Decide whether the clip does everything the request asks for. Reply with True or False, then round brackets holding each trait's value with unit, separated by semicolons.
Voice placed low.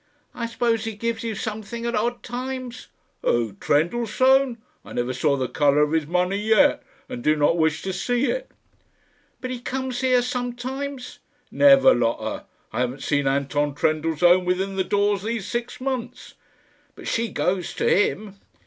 False (215 Hz)